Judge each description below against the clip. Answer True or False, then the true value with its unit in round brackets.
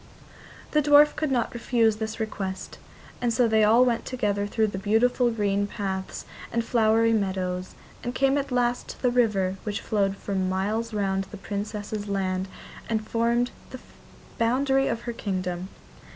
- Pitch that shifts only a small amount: False (3.4 semitones)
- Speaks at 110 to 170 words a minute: True (160 wpm)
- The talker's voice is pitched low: False (220 Hz)